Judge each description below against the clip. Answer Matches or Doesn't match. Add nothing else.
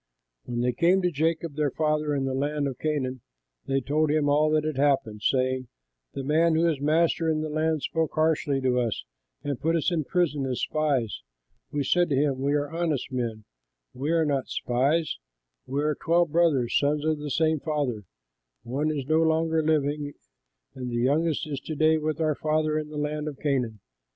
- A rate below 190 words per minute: Doesn't match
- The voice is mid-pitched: Matches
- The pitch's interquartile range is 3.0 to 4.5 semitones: Doesn't match